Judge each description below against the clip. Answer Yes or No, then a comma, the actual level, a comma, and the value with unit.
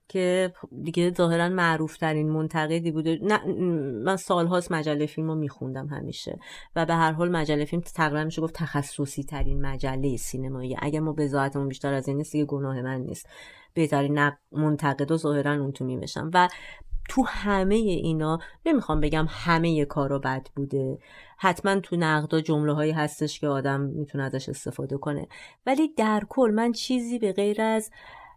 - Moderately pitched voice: Yes, medium, 155 Hz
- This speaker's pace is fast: Yes, fast, 165 wpm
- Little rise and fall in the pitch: No, average, 3.6 semitones